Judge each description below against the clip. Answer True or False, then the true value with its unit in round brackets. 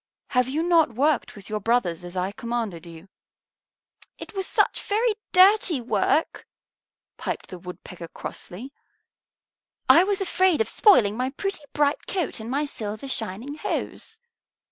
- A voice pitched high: True (250 Hz)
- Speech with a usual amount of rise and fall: False (8.7 semitones)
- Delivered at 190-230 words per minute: False (145 wpm)